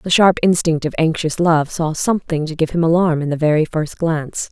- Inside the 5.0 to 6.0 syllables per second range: Yes, 5.4 syllables/s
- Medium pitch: Yes, medium, 160 Hz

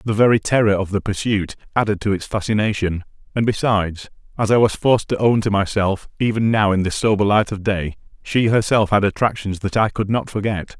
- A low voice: Yes, low, 105 Hz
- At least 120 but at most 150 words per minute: No, fast, 205 wpm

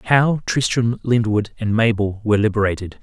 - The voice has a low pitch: Yes, low, 110 Hz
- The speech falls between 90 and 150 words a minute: Yes, average, 140 wpm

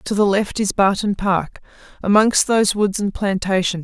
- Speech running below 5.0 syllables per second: Yes, 4.8 syllables/s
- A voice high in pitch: Yes, high, 200 Hz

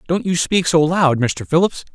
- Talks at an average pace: No, fast, 215 wpm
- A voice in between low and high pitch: Yes, medium, 160 Hz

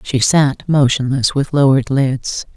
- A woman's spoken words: Yes, female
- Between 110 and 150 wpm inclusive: Yes, average, 140 wpm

